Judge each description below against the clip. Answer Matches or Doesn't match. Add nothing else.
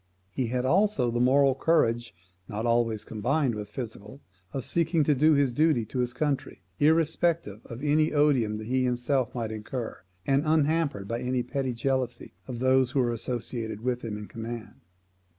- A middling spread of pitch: Matches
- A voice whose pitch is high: Doesn't match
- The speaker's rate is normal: Matches